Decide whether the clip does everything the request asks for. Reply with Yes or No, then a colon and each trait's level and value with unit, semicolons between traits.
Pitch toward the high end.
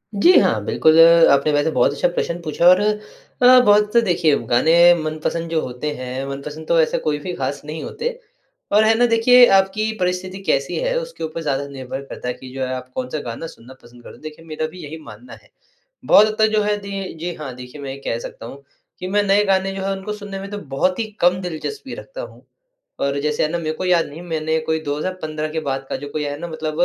No: medium, 160 Hz